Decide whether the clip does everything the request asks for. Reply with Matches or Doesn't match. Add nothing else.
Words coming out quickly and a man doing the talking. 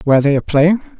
Matches